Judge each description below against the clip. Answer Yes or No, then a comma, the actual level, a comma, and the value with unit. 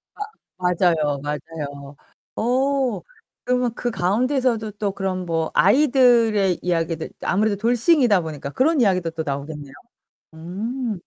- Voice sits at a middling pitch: No, high, 195 Hz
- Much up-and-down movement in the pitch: Yes, wide, 6.9 semitones